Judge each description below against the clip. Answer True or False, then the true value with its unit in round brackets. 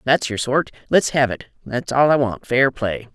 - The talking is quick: True (230 wpm)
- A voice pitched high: False (125 Hz)